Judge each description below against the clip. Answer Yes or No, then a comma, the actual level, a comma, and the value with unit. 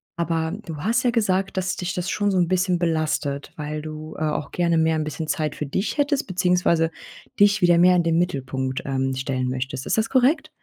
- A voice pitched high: No, medium, 170 Hz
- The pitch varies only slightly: No, average, 3.6 semitones